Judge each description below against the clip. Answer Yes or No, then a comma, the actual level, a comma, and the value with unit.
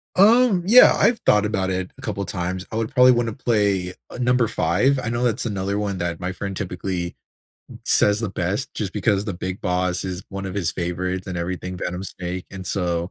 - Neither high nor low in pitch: No, very low, 95 Hz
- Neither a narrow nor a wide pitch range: Yes, average, 3.7 semitones